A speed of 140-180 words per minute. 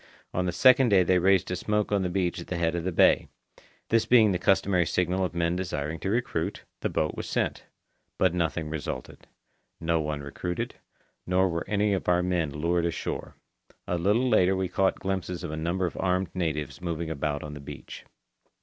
No: average, 200 wpm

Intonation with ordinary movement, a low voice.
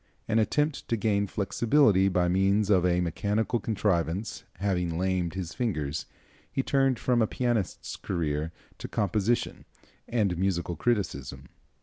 Yes: average, 4.2 semitones; very low, 95 Hz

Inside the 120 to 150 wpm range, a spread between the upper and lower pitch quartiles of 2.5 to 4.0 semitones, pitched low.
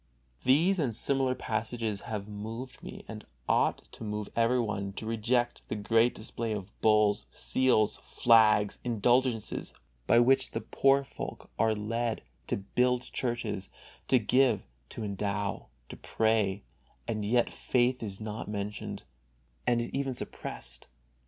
Yes: slow, 135 wpm; average, 2.8 semitones; low, 115 Hz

